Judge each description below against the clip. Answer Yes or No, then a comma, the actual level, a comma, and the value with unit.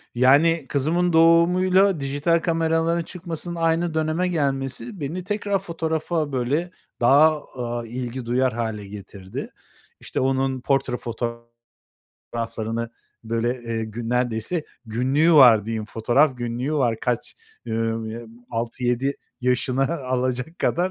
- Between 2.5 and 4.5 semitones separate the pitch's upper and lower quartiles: No, wide, 5.5 semitones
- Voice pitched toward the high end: No, low, 135 Hz